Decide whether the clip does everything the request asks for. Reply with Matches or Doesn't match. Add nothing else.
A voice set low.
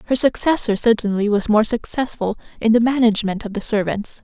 Doesn't match